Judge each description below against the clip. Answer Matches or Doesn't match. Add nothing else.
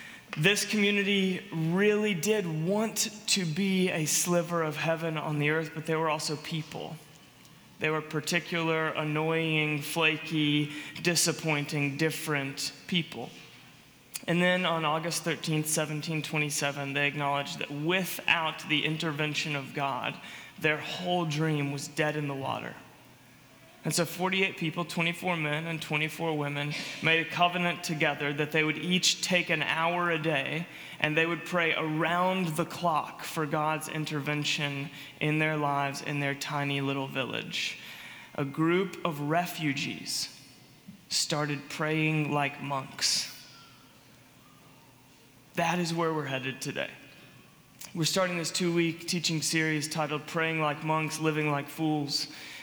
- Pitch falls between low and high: Matches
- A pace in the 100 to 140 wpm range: Matches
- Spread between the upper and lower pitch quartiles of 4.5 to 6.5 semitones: Doesn't match